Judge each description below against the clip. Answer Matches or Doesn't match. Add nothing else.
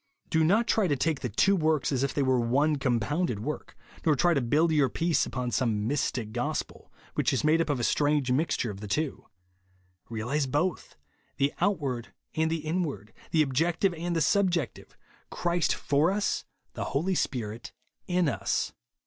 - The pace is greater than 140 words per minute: Matches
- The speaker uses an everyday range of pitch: Matches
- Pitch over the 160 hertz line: Doesn't match